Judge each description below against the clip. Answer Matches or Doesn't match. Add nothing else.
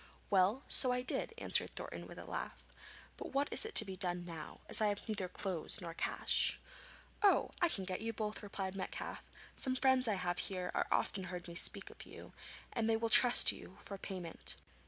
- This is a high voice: Matches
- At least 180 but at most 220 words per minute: Matches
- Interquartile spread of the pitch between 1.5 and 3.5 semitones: Doesn't match